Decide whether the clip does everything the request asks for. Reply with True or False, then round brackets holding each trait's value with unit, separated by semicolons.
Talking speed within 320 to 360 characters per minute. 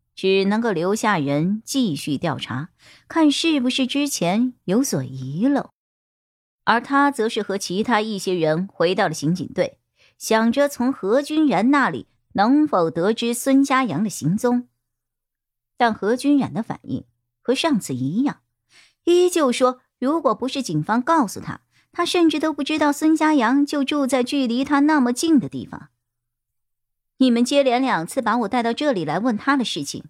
False (235 characters per minute)